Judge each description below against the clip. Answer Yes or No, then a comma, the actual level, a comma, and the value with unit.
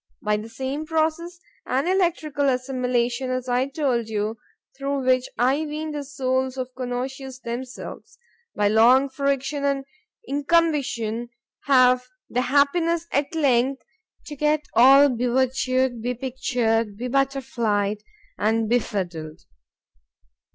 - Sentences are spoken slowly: Yes, slow, 115 wpm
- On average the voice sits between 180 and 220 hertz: No, very high, 260 Hz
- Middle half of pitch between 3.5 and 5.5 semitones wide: No, average, 2.8 semitones